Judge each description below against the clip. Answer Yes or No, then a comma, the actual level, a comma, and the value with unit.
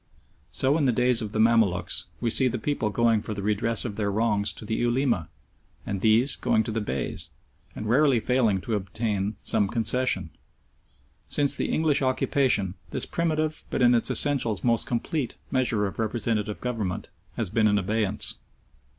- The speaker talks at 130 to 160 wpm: No, average, 170 wpm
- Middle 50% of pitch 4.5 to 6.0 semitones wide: No, average, 3.3 semitones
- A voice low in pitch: Yes, low, 115 Hz